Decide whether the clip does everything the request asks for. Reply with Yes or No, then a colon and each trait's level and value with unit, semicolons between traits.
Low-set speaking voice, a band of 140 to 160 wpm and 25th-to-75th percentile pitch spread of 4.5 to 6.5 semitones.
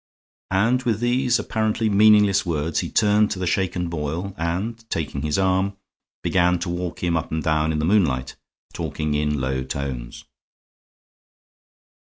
Yes: very low, 90 Hz; average, 150 wpm; average, 5.2 semitones